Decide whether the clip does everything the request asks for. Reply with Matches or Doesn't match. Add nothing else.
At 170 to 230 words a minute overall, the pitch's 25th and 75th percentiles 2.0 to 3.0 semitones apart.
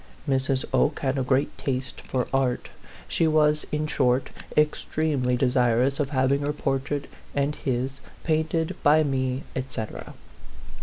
Doesn't match